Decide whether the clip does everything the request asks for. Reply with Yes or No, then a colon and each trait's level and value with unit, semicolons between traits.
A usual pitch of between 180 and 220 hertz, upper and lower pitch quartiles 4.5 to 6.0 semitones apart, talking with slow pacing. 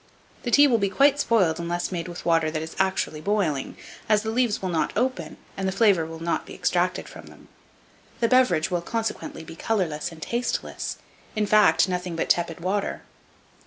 No: medium, 185 Hz; average, 4.9 semitones; average, 185 wpm